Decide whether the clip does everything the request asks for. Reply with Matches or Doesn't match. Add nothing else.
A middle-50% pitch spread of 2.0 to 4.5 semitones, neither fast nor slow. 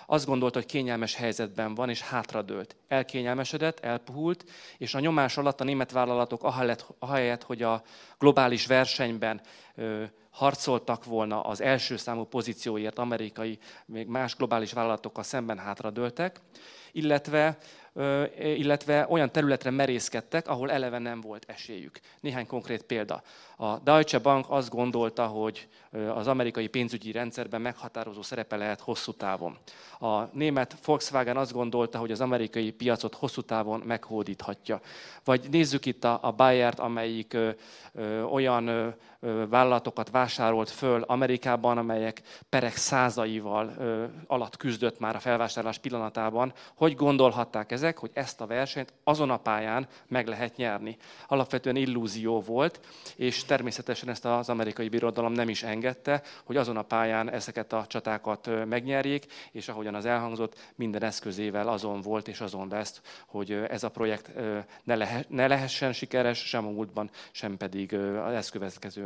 Matches